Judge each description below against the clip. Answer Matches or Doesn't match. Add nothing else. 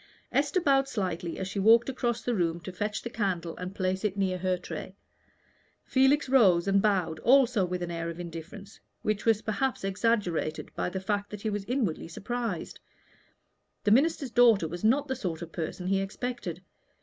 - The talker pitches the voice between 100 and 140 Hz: Doesn't match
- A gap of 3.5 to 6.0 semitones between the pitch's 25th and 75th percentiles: Matches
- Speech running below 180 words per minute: Doesn't match